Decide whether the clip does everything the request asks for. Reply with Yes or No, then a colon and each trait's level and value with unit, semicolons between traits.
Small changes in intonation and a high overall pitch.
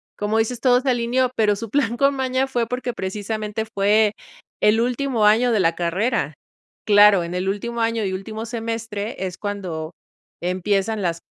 No: average, 3.1 semitones; high, 220 Hz